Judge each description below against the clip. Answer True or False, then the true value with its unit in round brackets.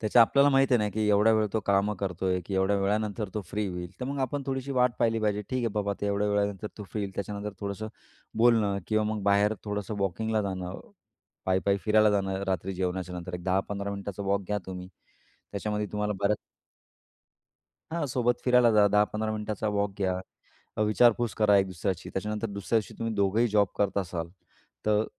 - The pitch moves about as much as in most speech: False (1.8 semitones)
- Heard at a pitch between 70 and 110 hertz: True (105 Hz)